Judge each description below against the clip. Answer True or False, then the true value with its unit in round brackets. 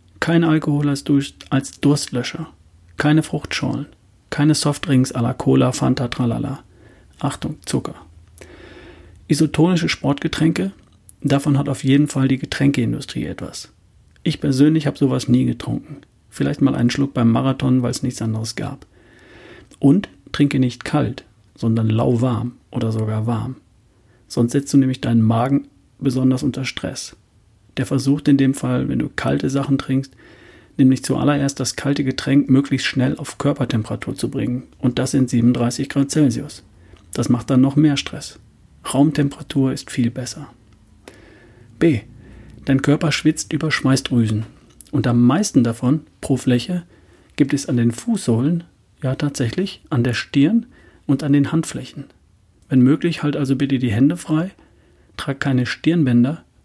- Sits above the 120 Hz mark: True (135 Hz)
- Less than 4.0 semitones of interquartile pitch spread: True (3.3 semitones)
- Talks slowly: False (140 wpm)